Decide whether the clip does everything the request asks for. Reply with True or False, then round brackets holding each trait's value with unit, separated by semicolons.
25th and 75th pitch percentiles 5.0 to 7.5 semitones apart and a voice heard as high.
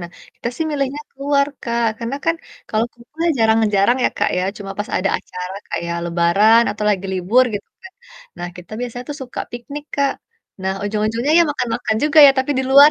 True (5.3 semitones; 235 Hz)